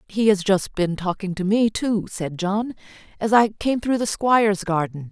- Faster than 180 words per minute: Yes, average, 200 wpm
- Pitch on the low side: No, high, 205 Hz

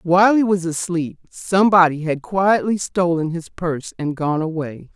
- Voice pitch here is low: No, medium, 175 Hz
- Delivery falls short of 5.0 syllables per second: Yes, 4.7 syllables/s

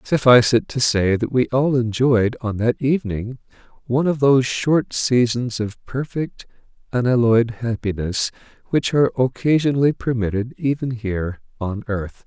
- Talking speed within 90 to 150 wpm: Yes, slow, 135 wpm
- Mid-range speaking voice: No, low, 120 Hz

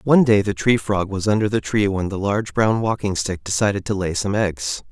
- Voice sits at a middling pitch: No, low, 100 Hz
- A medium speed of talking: No, fast, 245 wpm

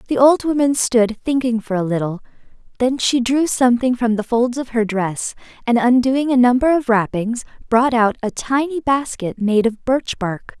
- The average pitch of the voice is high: Yes, high, 240 Hz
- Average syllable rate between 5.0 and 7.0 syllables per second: No, 4.7 syllables/s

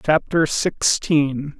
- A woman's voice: No, male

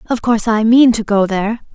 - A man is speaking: No, female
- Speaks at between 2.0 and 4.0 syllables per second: No, 6.1 syllables/s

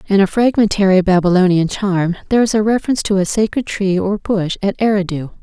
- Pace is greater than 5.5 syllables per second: Yes, 6.0 syllables/s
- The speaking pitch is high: Yes, high, 195 Hz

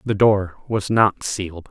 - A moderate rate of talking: Yes, average, 175 wpm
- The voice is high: No, low, 100 Hz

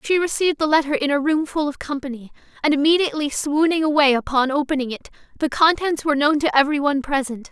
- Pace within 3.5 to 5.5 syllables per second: No, 6.6 syllables/s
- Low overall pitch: No, very high, 290 Hz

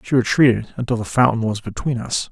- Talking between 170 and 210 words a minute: Yes, fast, 205 wpm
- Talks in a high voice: No, low, 120 Hz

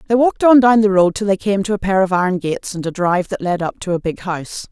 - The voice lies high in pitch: Yes, high, 195 Hz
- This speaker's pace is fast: Yes, fast, 320 wpm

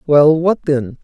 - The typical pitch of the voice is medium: Yes, medium, 150 Hz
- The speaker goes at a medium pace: Yes, average, 175 wpm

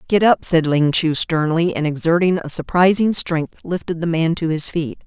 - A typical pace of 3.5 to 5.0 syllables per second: Yes, 4.8 syllables/s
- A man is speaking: No, female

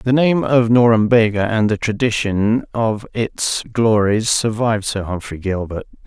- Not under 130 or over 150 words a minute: Yes, average, 140 wpm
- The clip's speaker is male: Yes, male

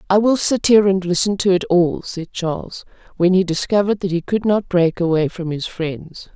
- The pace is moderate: No, fast, 215 wpm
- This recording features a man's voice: No, female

